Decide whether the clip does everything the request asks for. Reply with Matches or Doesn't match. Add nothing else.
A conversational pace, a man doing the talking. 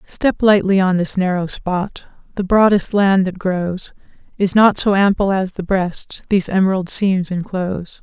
Doesn't match